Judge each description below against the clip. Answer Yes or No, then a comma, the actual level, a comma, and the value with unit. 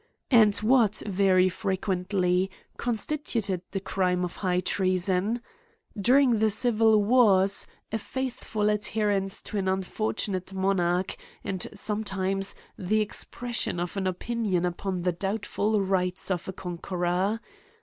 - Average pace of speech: No, slow, 120 wpm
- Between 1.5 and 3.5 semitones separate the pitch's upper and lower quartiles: Yes, average, 2.7 semitones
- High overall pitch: Yes, high, 195 Hz